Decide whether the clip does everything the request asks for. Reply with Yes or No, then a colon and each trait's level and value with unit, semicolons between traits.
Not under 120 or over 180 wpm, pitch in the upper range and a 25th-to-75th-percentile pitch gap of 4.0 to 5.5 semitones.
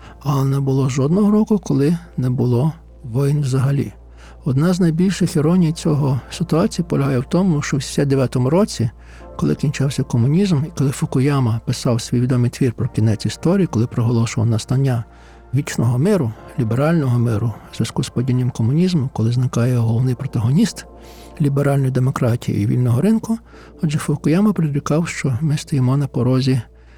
No: average, 145 wpm; low, 135 Hz; average, 4.3 semitones